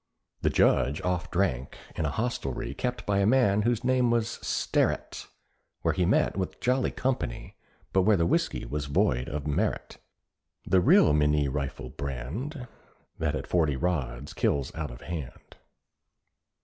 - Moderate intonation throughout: No, wide, 7.5 semitones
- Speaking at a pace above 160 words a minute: No, average, 150 wpm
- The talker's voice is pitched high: No, very low, 85 Hz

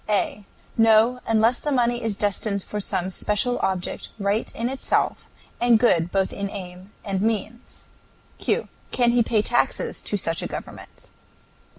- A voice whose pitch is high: Yes, high, 215 Hz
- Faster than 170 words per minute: No, average, 155 wpm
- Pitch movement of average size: Yes, average, 3.2 semitones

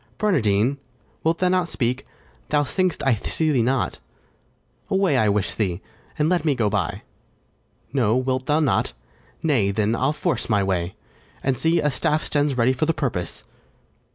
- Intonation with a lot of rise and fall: Yes, wide, 6.0 semitones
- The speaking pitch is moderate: No, low, 130 Hz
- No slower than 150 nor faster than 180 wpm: Yes, average, 165 wpm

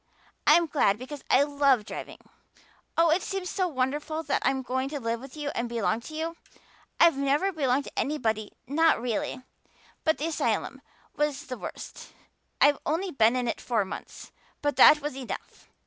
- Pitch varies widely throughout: No, average, 3.7 semitones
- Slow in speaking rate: No, average, 175 wpm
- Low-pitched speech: No, very high, 280 Hz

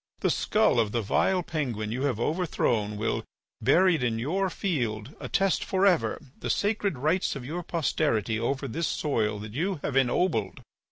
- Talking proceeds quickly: No, average, 165 wpm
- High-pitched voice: No, medium, 140 Hz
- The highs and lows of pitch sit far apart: Yes, wide, 7.7 semitones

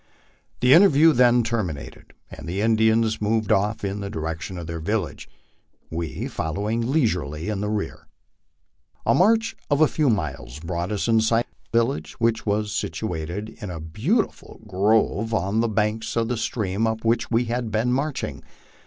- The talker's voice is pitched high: No, low, 110 Hz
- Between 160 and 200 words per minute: Yes, average, 170 wpm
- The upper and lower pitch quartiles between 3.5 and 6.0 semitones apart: Yes, average, 4.1 semitones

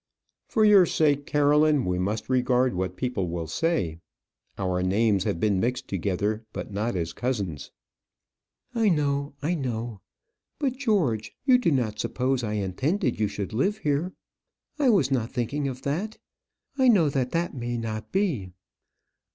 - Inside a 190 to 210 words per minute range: No, average, 155 wpm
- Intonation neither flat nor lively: No, wide, 6.8 semitones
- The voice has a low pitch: Yes, low, 125 Hz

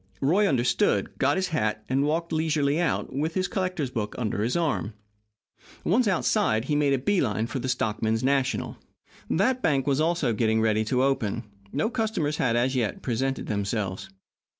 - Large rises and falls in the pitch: Yes, wide, 6.2 semitones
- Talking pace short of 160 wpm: No, average, 175 wpm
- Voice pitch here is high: No, low, 135 Hz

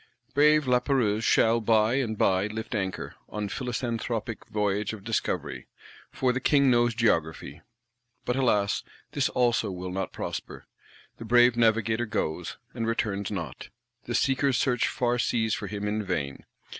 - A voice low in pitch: Yes, low, 115 Hz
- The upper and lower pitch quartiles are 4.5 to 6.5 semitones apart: No, average, 3.2 semitones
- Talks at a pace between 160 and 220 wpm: No, average, 145 wpm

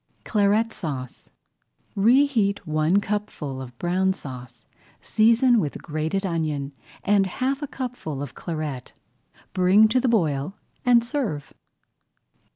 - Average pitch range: No, wide, 7.0 semitones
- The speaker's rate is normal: No, slow, 115 wpm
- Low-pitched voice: No, high, 190 Hz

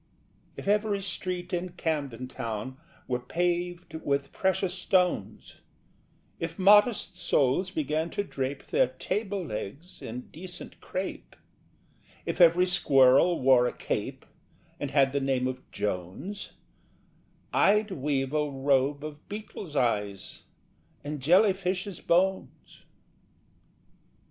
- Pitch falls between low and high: Yes, medium, 160 Hz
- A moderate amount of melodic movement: No, wide, 5.7 semitones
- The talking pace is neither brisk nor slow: No, slow, 110 wpm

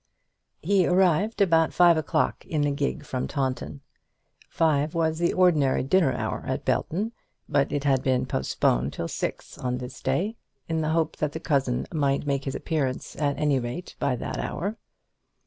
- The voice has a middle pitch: Yes, medium, 150 Hz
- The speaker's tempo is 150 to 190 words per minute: Yes, average, 170 wpm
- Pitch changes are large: No, average, 4.0 semitones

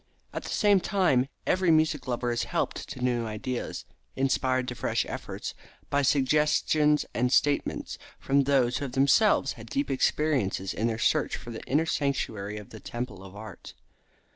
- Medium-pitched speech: No, low, 130 Hz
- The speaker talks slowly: No, average, 165 wpm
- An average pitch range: Yes, average, 3.9 semitones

